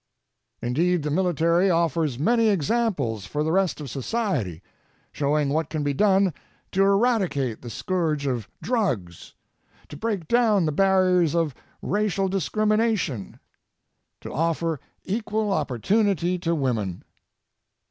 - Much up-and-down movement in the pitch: Yes, wide, 5.7 semitones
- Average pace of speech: No, slow, 120 wpm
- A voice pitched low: No, medium, 170 Hz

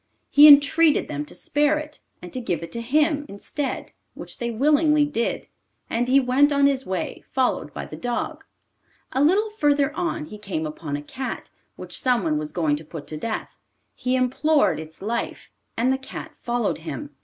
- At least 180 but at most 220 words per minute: Yes, average, 185 wpm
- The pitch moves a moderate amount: No, wide, 7.1 semitones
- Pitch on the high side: Yes, very high, 255 Hz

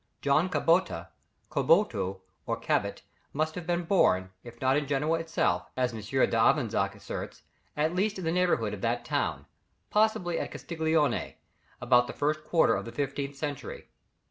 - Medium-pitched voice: Yes, medium, 150 Hz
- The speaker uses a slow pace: No, average, 155 wpm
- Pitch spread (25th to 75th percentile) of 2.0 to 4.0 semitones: No, average, 5.2 semitones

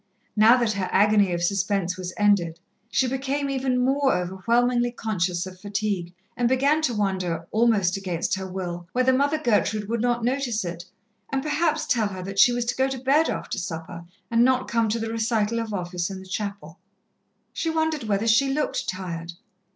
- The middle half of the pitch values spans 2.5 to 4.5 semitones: No, average, 5.2 semitones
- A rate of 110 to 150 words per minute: No, average, 185 wpm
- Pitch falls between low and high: No, high, 215 Hz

